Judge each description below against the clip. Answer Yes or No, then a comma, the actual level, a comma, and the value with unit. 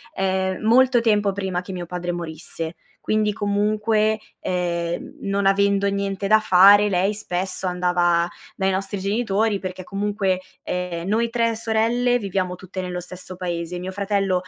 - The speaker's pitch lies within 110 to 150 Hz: No, high, 195 Hz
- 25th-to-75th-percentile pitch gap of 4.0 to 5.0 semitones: No, narrow, 2.6 semitones